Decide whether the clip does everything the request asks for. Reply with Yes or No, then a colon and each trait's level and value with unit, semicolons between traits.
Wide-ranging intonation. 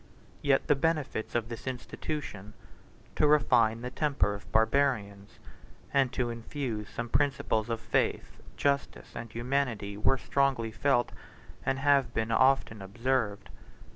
No: average, 3.8 semitones